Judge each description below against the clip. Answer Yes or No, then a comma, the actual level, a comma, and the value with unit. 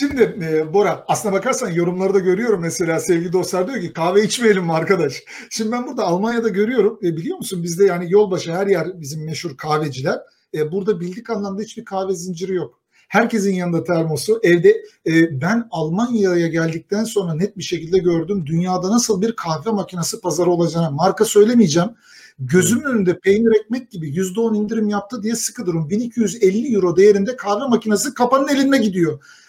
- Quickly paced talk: Yes, fast, 165 wpm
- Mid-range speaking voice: No, high, 195 Hz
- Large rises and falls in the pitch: No, average, 4.3 semitones